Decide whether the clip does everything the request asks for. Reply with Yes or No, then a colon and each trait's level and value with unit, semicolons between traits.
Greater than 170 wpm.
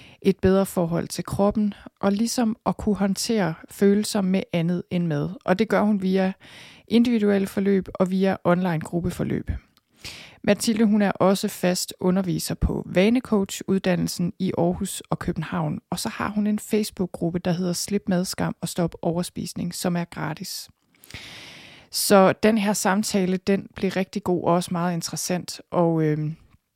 No: average, 155 wpm